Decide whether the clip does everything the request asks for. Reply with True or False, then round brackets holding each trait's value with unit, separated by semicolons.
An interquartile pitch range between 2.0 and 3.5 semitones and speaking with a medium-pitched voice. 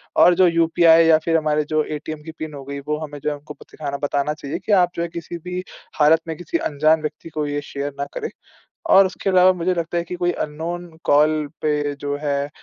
True (2.5 semitones; 155 Hz)